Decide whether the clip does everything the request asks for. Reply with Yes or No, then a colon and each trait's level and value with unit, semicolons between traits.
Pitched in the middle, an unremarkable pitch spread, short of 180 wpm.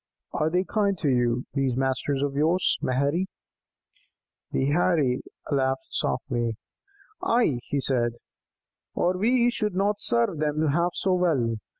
No: medium, 150 Hz; wide, 5.7 semitones; slow, 135 wpm